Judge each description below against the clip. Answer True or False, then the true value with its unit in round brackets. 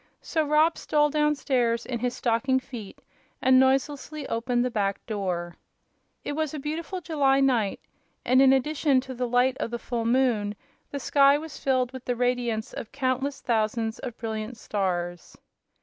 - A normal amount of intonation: True (3.3 semitones)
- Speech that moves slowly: False (165 wpm)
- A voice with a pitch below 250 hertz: False (255 Hz)